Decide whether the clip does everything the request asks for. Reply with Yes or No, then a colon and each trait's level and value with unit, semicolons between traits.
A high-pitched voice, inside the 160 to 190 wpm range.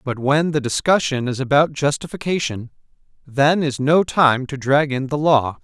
No: medium, 140 Hz; average, 170 wpm